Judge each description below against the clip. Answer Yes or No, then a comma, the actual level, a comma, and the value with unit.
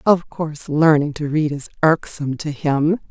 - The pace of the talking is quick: No, average, 175 wpm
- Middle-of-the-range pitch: Yes, medium, 150 Hz